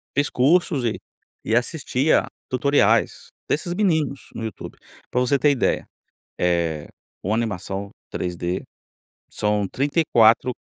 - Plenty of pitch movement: Yes, wide, 6.1 semitones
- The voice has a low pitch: Yes, low, 125 Hz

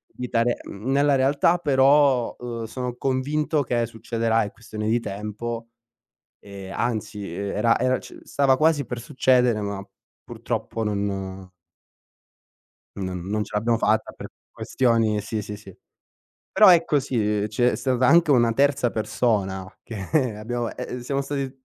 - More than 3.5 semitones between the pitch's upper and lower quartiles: Yes, average, 3.9 semitones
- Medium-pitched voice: No, low, 120 Hz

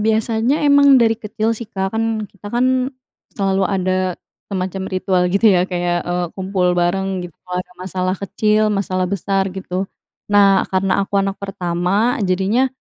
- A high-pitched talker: Yes, high, 195 Hz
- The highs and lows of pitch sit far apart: No, average, 2.8 semitones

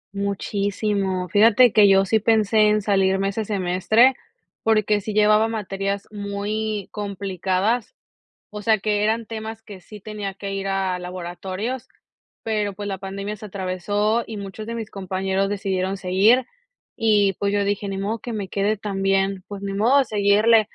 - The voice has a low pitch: No, high, 205 Hz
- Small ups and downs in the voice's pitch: Yes, narrow, 1.8 semitones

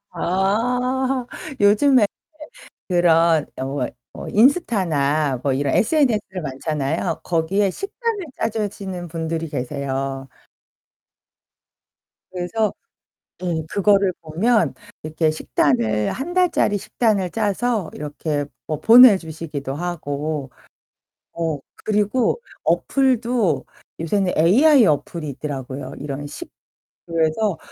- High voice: No, medium, 175 Hz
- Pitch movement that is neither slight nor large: No, wide, 6.6 semitones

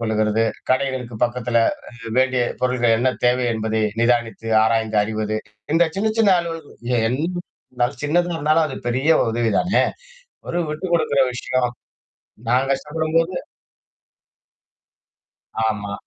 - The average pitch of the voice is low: Yes, low, 125 Hz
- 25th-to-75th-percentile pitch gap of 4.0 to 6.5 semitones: Yes, average, 5.0 semitones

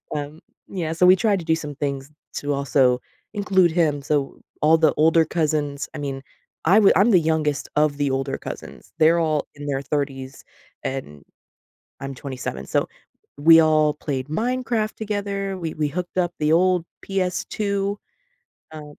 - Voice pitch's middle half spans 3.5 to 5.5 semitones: Yes, average, 4.2 semitones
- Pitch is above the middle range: No, medium, 155 Hz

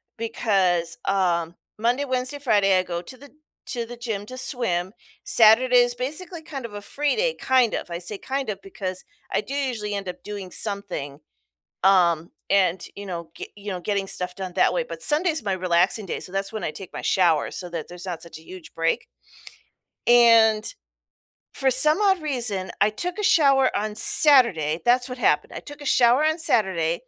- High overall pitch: Yes, high, 210 Hz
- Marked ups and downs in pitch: Yes, wide, 5.8 semitones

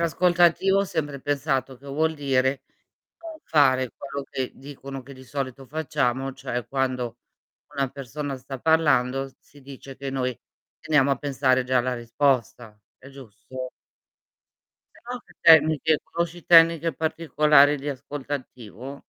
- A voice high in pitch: No, medium, 140 Hz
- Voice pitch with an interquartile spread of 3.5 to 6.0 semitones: No, average, 2.8 semitones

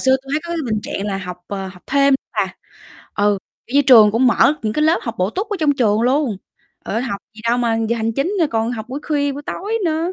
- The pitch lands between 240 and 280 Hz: Yes, high, 245 Hz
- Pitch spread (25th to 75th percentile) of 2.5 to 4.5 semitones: No, average, 5.1 semitones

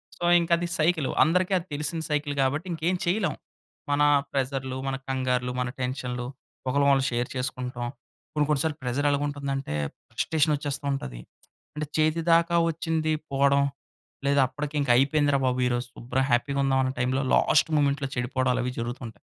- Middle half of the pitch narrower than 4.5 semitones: Yes, average, 2.9 semitones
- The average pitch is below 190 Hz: Yes, medium, 140 Hz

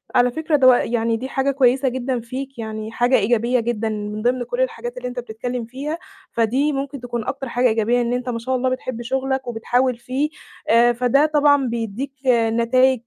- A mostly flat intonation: Yes, narrow, 2.3 semitones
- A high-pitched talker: Yes, high, 245 Hz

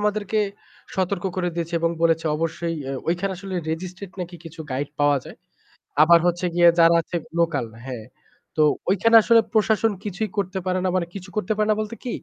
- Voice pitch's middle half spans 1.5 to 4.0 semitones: Yes, average, 3.5 semitones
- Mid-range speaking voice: Yes, medium, 180 Hz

